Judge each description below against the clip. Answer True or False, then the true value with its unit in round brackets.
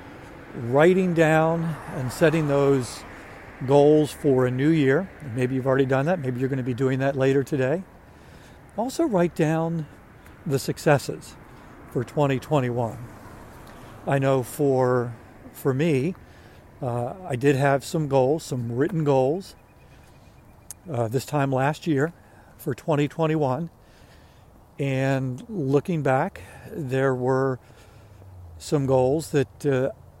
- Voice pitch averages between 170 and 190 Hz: False (135 Hz)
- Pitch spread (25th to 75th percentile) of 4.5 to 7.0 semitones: False (3.2 semitones)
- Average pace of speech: False (120 wpm)